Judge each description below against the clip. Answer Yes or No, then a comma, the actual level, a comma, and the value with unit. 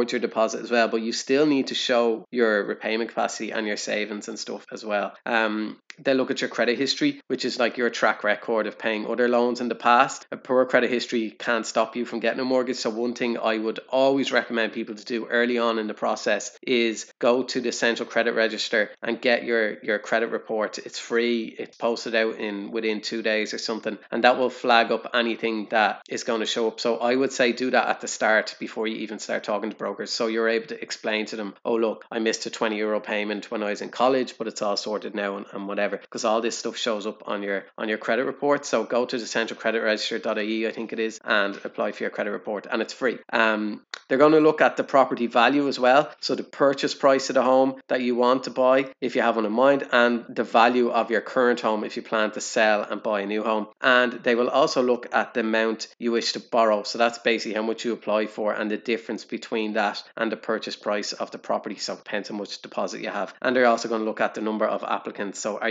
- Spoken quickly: Yes, fast, 250 wpm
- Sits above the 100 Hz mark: Yes, low, 115 Hz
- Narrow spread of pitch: Yes, narrow, 2.0 semitones